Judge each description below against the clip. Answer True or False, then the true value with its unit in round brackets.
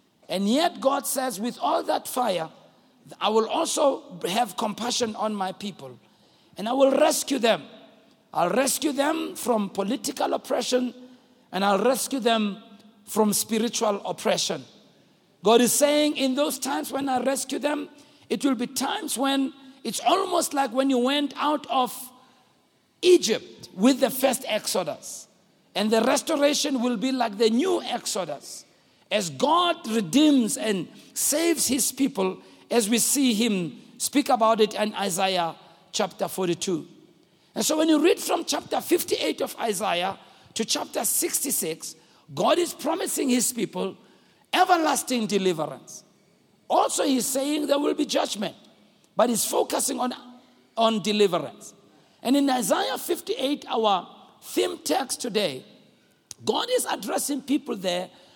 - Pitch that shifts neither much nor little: True (4.6 semitones)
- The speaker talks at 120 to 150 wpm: True (140 wpm)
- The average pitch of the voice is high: True (255 Hz)